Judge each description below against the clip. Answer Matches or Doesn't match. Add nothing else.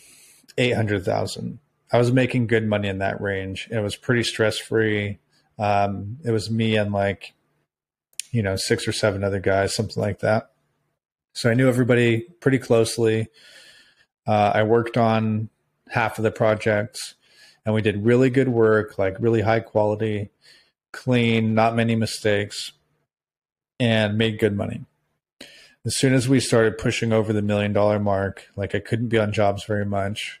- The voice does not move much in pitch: Matches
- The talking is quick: Doesn't match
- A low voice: Matches